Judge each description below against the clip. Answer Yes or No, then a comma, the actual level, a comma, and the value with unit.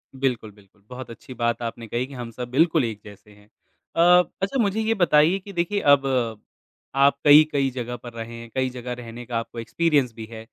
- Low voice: Yes, low, 125 Hz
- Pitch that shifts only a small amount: No, average, 4.9 semitones